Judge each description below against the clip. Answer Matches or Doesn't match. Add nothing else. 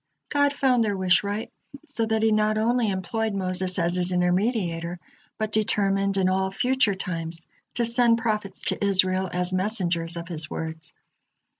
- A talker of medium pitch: Doesn't match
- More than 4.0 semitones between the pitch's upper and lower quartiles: Doesn't match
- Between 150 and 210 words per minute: Matches